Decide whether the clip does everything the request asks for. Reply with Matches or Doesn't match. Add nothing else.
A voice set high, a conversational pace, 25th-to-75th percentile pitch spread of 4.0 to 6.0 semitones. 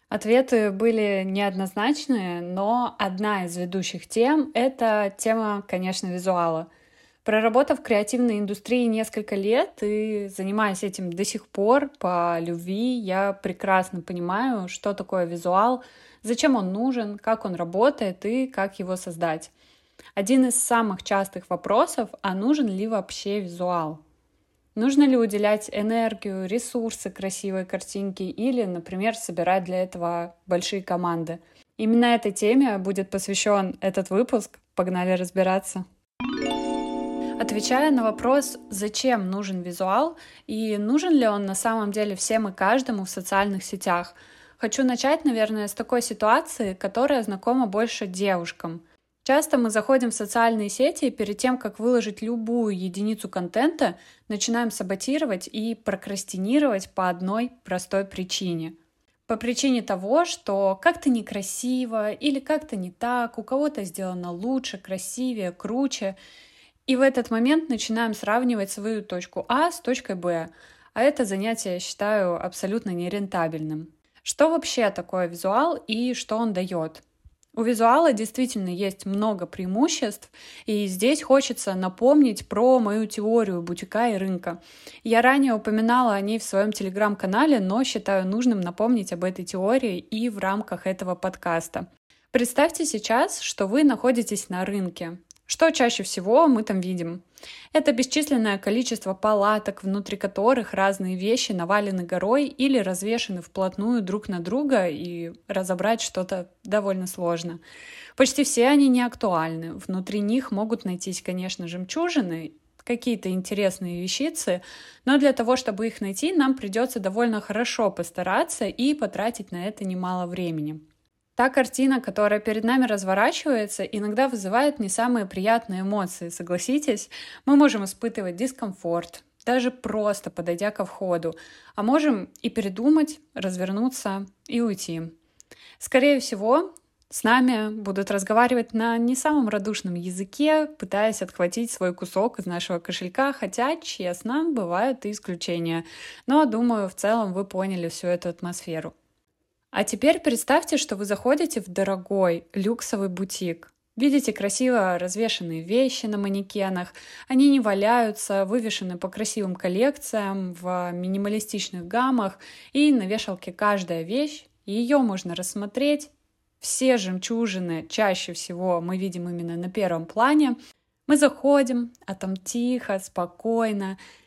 Matches